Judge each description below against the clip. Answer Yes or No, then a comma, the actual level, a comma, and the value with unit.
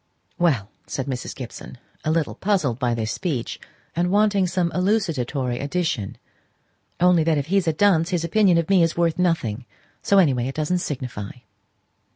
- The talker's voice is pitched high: No, medium, 165 Hz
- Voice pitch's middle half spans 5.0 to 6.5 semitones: Yes, wide, 5.6 semitones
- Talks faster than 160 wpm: Yes, average, 170 wpm